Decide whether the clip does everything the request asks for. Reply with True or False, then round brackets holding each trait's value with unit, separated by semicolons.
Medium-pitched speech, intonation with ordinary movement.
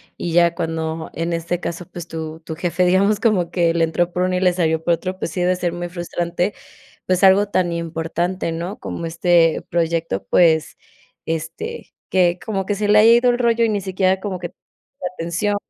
False (175 Hz; 2.2 semitones)